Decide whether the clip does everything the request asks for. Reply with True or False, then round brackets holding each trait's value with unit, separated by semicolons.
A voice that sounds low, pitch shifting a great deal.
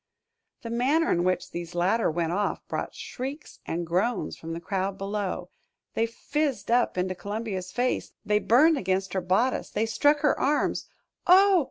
False (210 Hz; 5.8 semitones)